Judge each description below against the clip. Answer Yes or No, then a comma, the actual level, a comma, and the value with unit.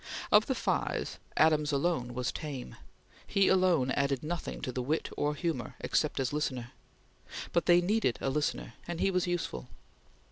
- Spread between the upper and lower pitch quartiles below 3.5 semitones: No, average, 5.0 semitones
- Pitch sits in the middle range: Yes, medium, 150 Hz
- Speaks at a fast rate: No, average, 170 wpm